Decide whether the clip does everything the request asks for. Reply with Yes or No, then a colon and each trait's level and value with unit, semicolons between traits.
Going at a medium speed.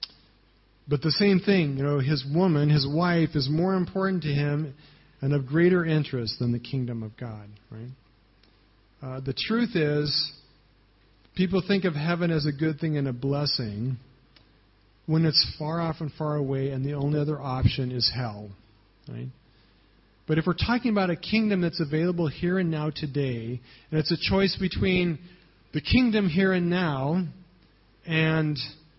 Yes: average, 165 wpm